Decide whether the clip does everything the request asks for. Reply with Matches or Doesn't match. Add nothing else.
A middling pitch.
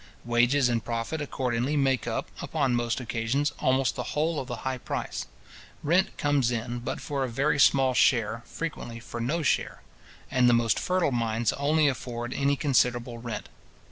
Doesn't match